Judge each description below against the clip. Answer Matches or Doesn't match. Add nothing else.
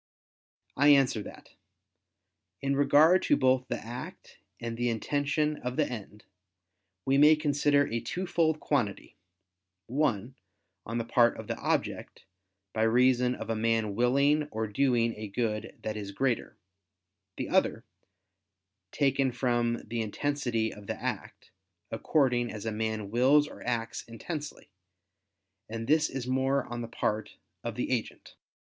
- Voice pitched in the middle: Doesn't match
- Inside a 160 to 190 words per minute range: Doesn't match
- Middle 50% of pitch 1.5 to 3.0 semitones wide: Doesn't match